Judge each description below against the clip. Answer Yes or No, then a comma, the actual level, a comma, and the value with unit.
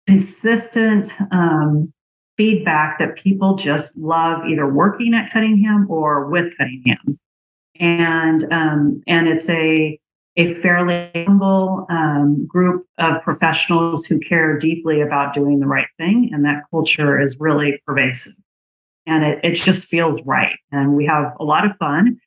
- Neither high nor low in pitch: Yes, medium, 165 Hz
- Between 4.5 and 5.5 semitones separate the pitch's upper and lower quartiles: No, average, 3.5 semitones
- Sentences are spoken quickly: No, average, 145 wpm